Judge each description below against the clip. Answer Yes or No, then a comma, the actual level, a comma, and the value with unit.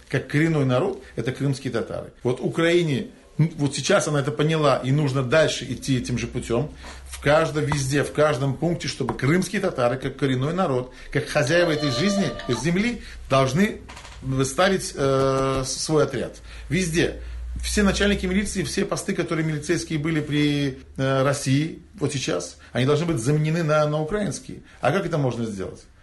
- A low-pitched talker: No, medium, 150 Hz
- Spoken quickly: Yes, fast, 160 wpm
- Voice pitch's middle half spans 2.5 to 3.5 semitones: No, average, 3.9 semitones